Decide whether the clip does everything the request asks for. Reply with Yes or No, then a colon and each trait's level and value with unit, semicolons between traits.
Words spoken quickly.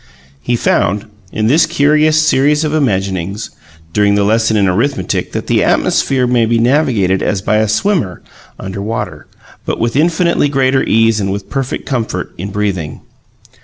No: average, 160 wpm